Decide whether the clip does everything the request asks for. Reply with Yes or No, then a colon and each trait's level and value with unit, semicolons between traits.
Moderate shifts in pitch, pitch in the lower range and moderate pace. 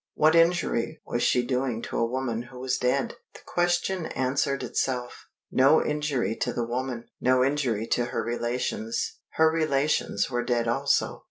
Yes: average, 3.6 semitones; low, 130 Hz; average, 160 wpm